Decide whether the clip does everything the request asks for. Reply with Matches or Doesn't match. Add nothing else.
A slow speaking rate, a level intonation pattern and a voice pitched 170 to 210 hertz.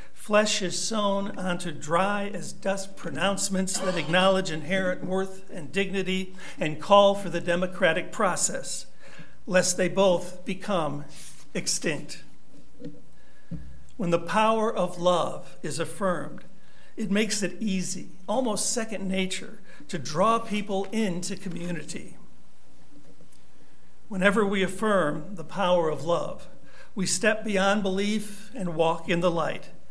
Matches